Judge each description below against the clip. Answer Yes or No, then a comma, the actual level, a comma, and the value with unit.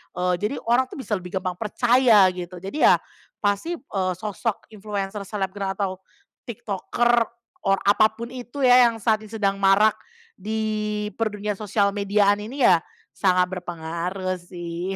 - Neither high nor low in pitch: No, high, 205 Hz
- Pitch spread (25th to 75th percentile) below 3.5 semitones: Yes, average, 2.7 semitones